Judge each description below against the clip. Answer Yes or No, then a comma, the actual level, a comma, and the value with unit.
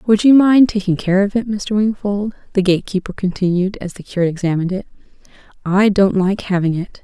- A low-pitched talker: No, high, 195 Hz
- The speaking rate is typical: Yes, average, 195 wpm